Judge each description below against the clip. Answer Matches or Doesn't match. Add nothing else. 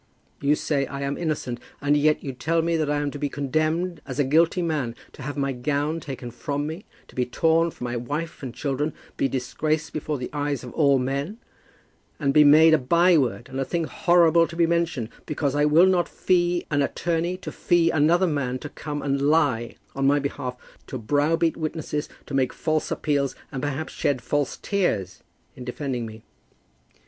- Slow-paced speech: Doesn't match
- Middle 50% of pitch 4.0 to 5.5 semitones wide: Doesn't match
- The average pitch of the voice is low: Doesn't match